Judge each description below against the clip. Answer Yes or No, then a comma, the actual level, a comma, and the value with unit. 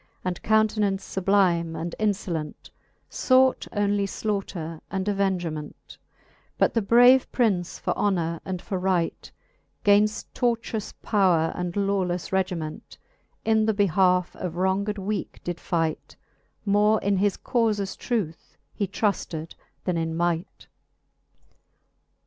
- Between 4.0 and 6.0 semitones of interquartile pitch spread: No, average, 3.1 semitones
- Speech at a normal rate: No, slow, 115 wpm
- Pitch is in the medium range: No, high, 195 Hz